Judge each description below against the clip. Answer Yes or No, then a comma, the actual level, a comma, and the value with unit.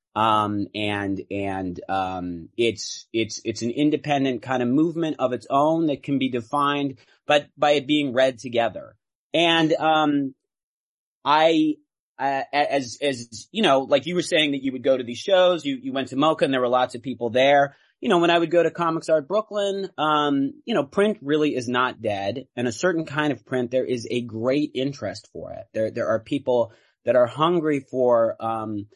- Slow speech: No, average, 200 wpm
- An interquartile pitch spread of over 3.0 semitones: Yes, average, 4.4 semitones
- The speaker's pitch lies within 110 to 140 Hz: Yes, low, 135 Hz